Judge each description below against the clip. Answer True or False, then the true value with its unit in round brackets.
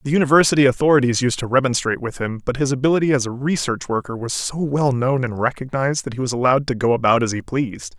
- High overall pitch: False (130 Hz)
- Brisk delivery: True (235 wpm)